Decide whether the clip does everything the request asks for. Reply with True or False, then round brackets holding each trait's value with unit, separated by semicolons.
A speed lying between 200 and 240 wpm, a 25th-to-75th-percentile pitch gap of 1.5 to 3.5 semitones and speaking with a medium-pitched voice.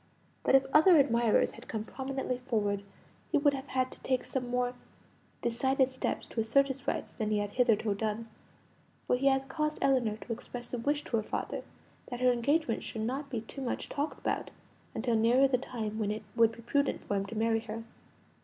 False (205 wpm; 3.1 semitones; 245 Hz)